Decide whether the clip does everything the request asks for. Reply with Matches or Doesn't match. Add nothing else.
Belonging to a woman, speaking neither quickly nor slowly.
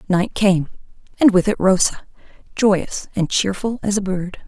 Matches